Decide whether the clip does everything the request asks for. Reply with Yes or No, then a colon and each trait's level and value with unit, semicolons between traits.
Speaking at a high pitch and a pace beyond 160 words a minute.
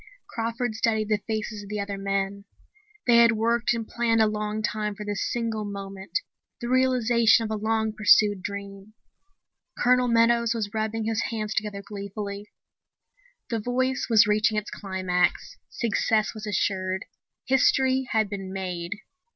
No: high, 215 Hz; average, 150 wpm